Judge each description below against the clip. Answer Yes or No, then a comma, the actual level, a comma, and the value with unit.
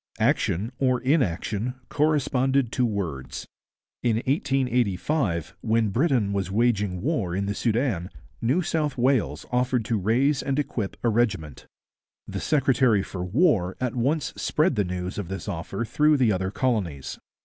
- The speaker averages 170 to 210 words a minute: No, average, 145 wpm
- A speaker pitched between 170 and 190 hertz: No, low, 115 Hz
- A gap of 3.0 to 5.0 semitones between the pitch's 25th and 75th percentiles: No, wide, 5.5 semitones